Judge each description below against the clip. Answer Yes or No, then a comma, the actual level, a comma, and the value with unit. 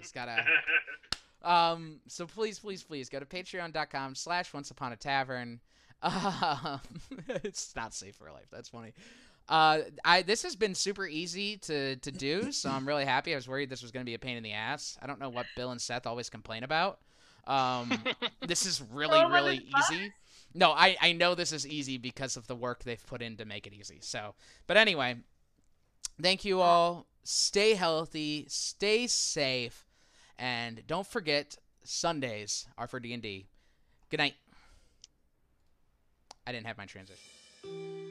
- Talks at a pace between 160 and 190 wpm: Yes, average, 170 wpm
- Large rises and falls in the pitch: Yes, wide, 6.2 semitones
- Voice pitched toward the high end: No, medium, 140 Hz